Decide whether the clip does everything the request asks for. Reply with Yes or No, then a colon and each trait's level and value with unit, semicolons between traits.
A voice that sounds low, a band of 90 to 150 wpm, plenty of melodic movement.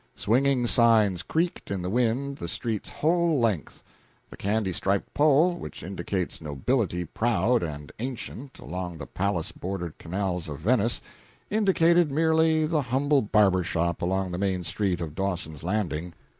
Yes: low, 100 Hz; average, 145 wpm; wide, 7.3 semitones